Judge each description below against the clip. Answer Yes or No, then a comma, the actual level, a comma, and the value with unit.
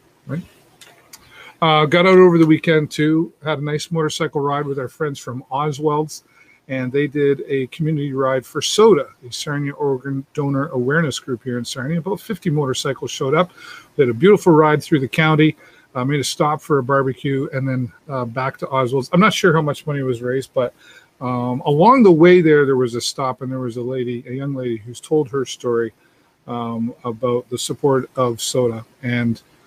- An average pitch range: Yes, average, 3.5 semitones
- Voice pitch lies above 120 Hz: Yes, medium, 140 Hz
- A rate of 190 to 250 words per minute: Yes, average, 200 wpm